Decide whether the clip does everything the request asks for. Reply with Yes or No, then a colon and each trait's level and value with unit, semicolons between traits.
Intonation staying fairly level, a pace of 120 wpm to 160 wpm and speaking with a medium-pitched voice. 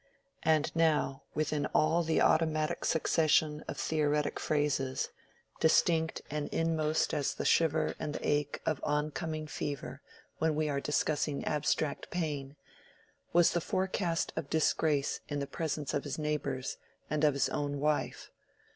Yes: narrow, 1.6 semitones; average, 140 wpm; medium, 150 Hz